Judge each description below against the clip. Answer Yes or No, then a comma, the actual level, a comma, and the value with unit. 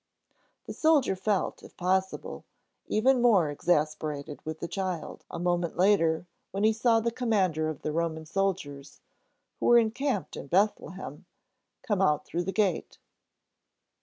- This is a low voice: No, medium, 185 Hz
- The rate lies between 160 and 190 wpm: No, average, 140 wpm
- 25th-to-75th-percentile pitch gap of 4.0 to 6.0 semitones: Yes, average, 5.2 semitones